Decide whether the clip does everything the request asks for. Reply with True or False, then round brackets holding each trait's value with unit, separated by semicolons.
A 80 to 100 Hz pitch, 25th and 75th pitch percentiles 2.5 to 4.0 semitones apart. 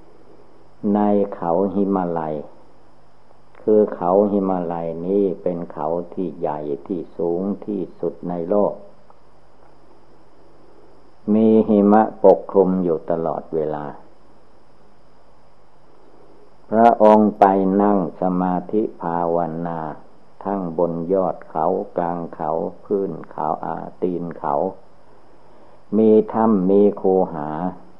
True (95 Hz; 3.1 semitones)